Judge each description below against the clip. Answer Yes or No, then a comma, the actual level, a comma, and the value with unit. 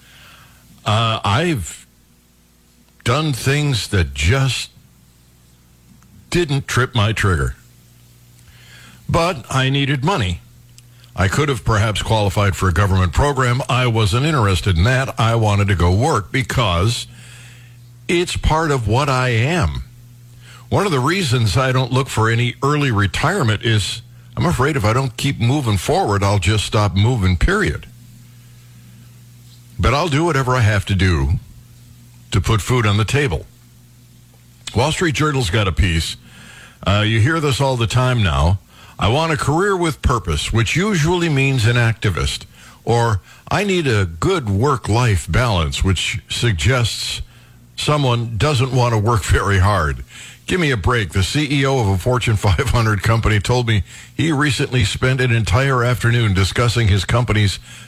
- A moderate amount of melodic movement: Yes, average, 4.0 semitones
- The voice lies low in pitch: Yes, low, 120 Hz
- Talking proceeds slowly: No, average, 150 wpm